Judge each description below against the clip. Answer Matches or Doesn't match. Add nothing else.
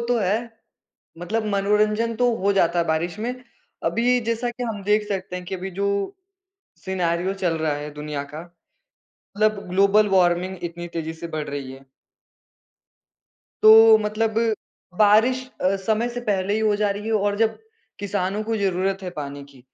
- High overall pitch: Matches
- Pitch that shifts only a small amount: Doesn't match